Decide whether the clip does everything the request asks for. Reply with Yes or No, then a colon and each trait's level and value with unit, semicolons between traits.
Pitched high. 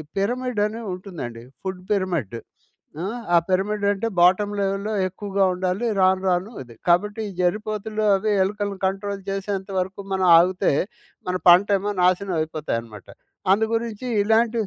Yes: high, 195 Hz